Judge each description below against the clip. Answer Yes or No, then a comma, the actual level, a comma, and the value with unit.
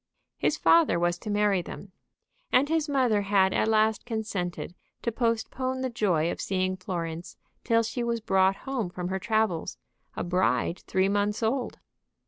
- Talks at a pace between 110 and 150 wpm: No, average, 160 wpm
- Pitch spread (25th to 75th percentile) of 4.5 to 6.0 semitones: No, average, 4.0 semitones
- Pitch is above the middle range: Yes, high, 210 Hz